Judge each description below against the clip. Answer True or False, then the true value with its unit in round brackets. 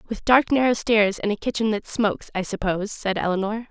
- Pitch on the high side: True (215 Hz)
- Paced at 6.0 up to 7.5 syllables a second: False (5.7 syllables/s)